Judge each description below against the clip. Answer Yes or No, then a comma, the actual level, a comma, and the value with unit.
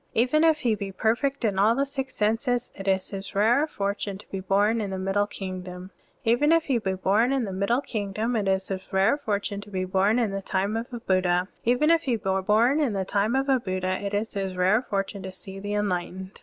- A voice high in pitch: Yes, high, 205 Hz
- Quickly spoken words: Yes, fast, 240 wpm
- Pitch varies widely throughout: No, average, 3.8 semitones